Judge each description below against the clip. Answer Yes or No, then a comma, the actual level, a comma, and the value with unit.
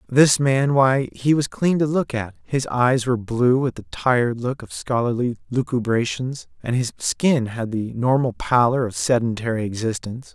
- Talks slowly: No, average, 170 wpm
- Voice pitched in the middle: No, low, 125 Hz